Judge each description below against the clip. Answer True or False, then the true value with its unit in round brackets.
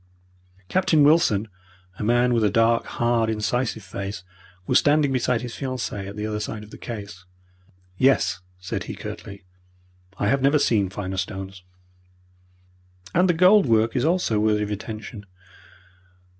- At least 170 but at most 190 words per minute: False (150 wpm)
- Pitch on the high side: False (110 Hz)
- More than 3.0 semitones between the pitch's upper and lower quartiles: True (4.1 semitones)